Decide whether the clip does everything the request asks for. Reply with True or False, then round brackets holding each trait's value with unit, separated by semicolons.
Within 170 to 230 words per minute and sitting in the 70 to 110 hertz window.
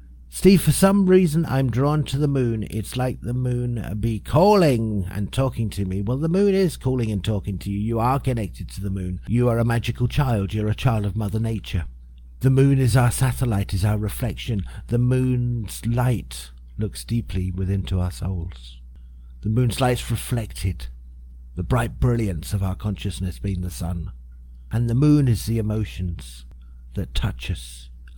True (180 wpm; 105 Hz)